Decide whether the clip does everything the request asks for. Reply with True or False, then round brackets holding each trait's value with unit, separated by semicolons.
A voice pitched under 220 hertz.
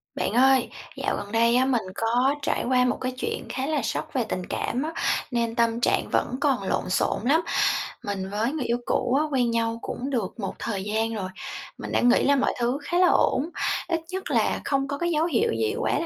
False (245 Hz)